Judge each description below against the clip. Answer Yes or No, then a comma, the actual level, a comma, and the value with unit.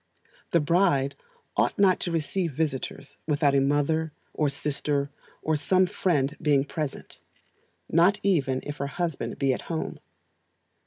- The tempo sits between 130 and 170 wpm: Yes, average, 140 wpm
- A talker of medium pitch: Yes, medium, 150 Hz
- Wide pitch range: No, average, 3.1 semitones